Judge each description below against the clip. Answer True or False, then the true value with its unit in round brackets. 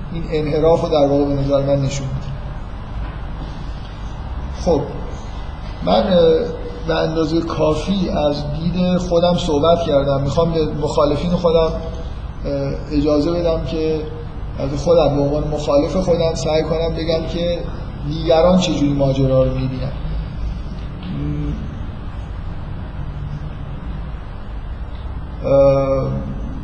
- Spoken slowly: True (90 wpm)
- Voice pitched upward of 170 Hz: False (145 Hz)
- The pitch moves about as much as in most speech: False (6.7 semitones)